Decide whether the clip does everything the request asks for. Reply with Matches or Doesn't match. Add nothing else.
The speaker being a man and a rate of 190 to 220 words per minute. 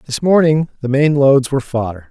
Matches